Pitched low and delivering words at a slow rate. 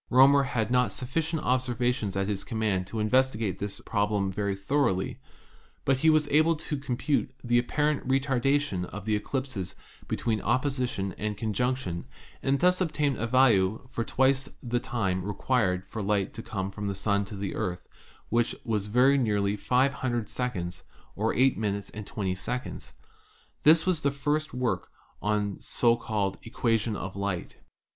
No: low, 115 Hz; average, 165 wpm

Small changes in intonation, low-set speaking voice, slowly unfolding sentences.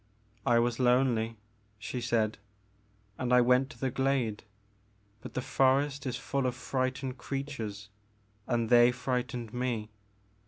Yes: narrow, 2.0 semitones; low, 125 Hz; slow, 130 wpm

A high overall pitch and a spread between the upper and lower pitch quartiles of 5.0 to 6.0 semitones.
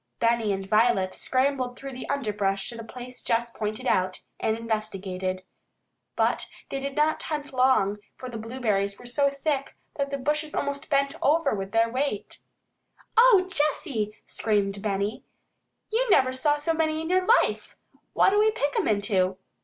Yes: very high, 250 Hz; average, 5.3 semitones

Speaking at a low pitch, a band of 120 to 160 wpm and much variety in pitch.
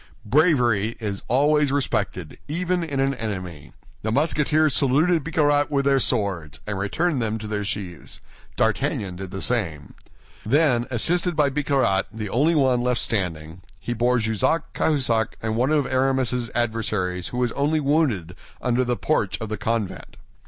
Yes: low, 120 Hz; average, 155 wpm; wide, 5.7 semitones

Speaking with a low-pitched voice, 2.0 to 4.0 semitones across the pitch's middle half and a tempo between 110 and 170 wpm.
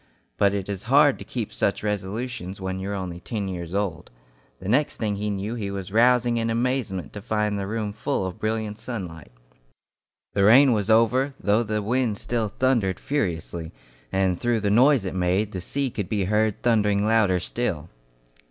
No: low, 105 Hz; average, 3.5 semitones; average, 185 wpm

